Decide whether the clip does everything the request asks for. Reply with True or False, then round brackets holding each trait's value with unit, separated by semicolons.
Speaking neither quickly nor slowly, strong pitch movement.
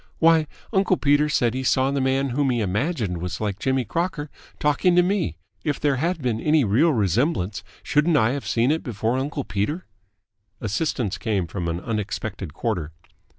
True (175 wpm; 6.2 semitones)